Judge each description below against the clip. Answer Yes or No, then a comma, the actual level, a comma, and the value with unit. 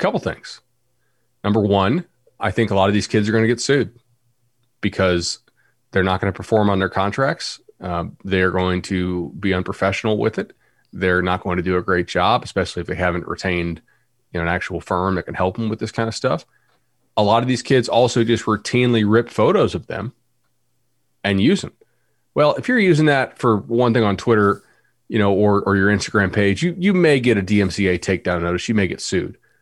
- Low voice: Yes, low, 105 Hz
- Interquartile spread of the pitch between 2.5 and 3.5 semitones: No, average, 4.1 semitones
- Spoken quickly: Yes, fast, 210 wpm